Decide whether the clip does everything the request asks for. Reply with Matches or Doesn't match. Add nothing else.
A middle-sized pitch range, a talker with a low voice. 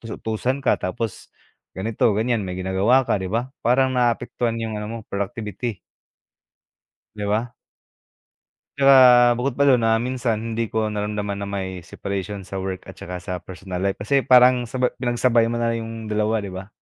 Matches